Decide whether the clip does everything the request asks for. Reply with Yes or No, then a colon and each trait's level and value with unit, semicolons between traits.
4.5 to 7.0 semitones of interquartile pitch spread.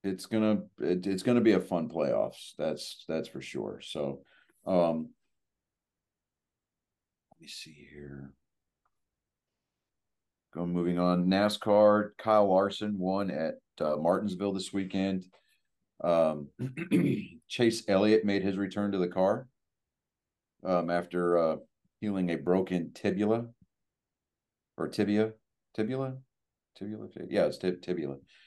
No: average, 3.2 semitones